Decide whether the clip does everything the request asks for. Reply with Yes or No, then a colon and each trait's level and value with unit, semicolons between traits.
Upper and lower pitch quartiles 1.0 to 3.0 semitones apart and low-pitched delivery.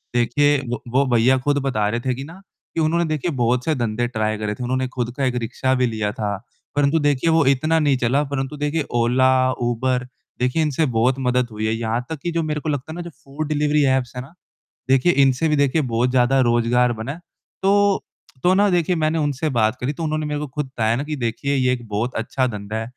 No: average, 3.8 semitones; low, 130 Hz